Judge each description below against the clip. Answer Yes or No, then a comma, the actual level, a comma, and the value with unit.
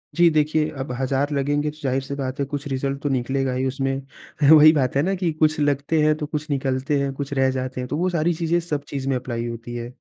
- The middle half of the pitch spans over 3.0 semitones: No, narrow, 2.5 semitones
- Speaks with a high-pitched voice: No, medium, 140 Hz